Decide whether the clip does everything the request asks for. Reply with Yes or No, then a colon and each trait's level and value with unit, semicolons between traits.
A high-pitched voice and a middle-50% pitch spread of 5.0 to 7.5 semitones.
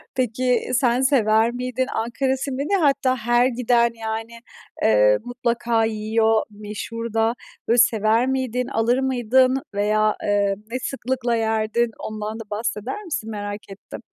No: high, 235 Hz; average, 2.8 semitones